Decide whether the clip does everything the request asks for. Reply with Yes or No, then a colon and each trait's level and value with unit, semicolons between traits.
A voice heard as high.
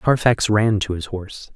No: low, 100 Hz